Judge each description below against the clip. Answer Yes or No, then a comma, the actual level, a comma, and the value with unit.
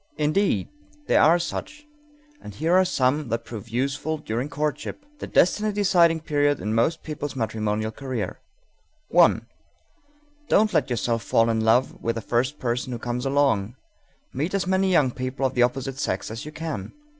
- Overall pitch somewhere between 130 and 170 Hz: Yes, low, 135 Hz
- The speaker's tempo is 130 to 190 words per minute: Yes, average, 170 wpm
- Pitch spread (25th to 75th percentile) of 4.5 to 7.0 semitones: Yes, average, 5.3 semitones